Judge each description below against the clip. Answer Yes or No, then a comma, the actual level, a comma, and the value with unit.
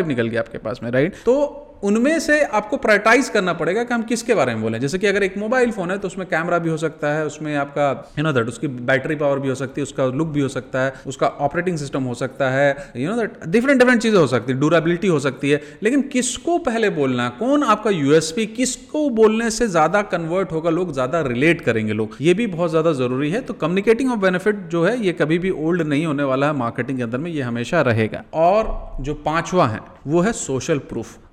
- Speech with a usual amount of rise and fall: No, wide, 7.6 semitones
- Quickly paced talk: Yes, fast, 235 wpm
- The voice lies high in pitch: No, medium, 160 Hz